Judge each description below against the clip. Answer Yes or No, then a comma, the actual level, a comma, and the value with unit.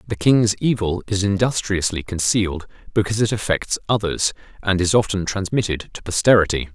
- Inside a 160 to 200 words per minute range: No, average, 140 wpm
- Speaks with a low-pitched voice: Yes, low, 100 Hz